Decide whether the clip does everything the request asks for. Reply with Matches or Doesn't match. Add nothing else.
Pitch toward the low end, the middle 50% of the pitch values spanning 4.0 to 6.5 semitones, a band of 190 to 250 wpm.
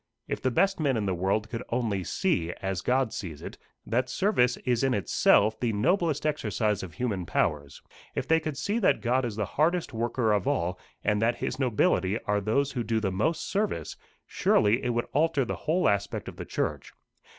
Matches